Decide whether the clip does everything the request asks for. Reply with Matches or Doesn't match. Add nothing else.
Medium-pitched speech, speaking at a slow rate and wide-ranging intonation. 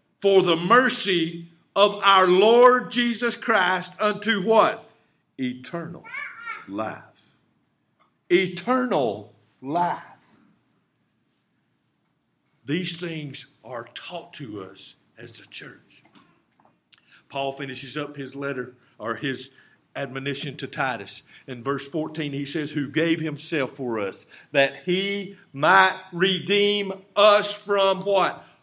Matches